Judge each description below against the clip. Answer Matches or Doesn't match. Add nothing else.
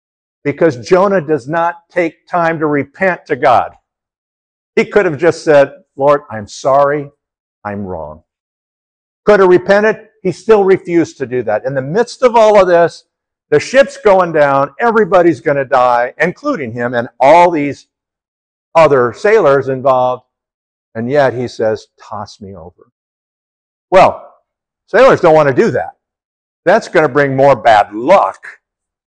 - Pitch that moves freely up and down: Matches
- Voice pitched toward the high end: Doesn't match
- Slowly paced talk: Doesn't match